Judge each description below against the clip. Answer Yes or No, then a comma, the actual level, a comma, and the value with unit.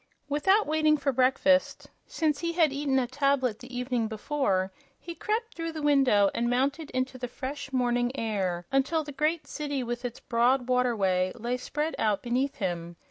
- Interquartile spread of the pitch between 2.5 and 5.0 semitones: Yes, average, 3.6 semitones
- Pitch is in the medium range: No, very high, 260 Hz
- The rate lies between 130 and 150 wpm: No, average, 175 wpm